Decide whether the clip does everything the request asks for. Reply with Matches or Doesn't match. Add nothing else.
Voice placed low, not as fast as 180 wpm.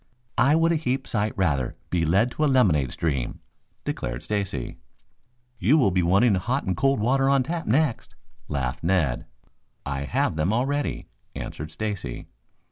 Matches